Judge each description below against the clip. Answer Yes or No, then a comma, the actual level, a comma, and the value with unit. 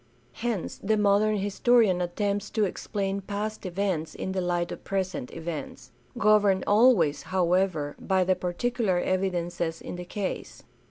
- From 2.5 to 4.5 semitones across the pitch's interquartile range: Yes, average, 2.8 semitones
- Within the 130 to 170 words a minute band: Yes, average, 140 wpm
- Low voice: No, high, 190 Hz